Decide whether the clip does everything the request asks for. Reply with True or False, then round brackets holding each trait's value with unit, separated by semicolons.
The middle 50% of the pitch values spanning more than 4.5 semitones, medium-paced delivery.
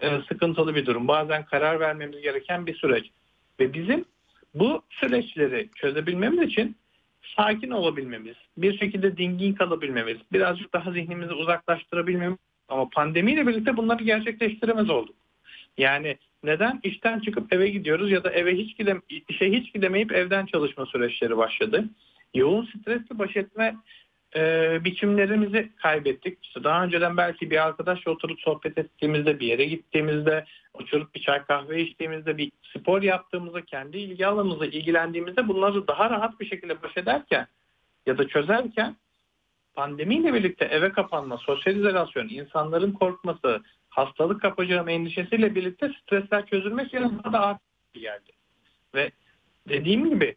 True (5.1 semitones; 130 wpm)